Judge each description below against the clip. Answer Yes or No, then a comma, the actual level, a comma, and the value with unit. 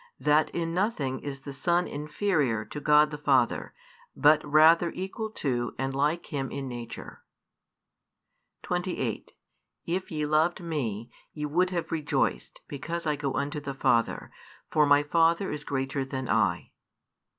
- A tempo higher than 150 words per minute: No, average, 145 wpm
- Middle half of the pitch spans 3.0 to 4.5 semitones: Yes, average, 3.5 semitones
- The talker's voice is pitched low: No, medium, 150 Hz